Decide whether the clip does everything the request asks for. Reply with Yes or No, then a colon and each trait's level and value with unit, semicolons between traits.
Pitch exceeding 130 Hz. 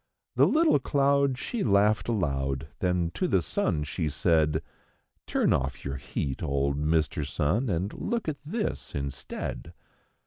No: very low, 85 Hz